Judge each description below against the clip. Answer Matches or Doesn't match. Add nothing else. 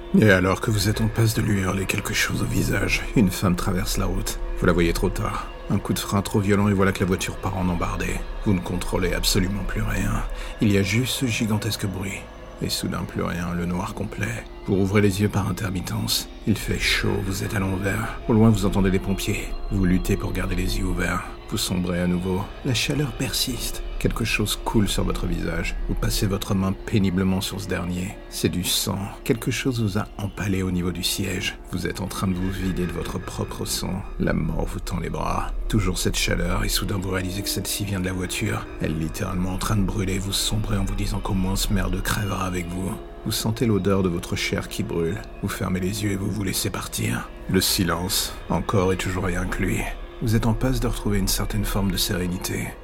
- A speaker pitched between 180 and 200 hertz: Doesn't match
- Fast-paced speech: Matches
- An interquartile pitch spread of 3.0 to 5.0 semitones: Doesn't match